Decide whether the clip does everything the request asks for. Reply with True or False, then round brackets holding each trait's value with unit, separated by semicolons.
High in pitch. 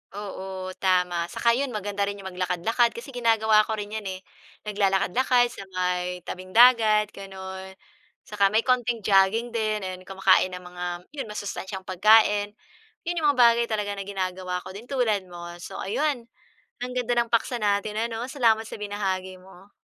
True (205 Hz)